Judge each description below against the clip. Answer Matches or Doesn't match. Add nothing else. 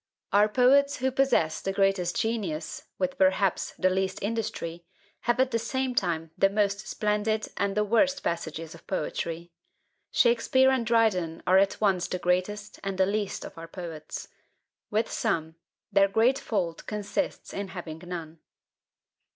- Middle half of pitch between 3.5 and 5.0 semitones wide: Matches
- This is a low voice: Doesn't match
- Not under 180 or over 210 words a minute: Doesn't match